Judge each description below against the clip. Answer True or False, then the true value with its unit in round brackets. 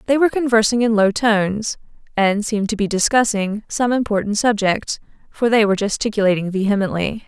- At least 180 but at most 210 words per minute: False (155 wpm)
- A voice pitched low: False (215 Hz)